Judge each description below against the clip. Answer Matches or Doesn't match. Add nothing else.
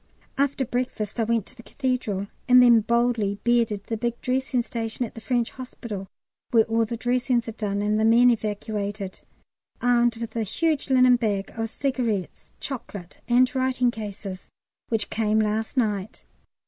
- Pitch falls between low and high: Doesn't match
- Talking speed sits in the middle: Matches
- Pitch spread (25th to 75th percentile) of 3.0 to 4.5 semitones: Doesn't match